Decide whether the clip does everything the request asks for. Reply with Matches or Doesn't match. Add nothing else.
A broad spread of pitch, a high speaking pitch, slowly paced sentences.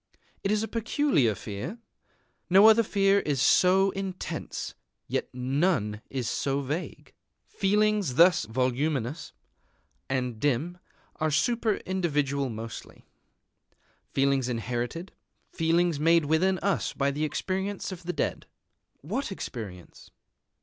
Doesn't match